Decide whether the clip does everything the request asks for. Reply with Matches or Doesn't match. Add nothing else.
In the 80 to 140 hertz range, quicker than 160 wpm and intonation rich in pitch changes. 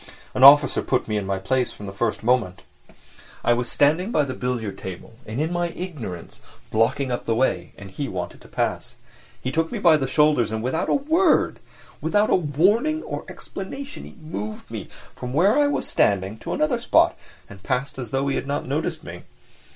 Matches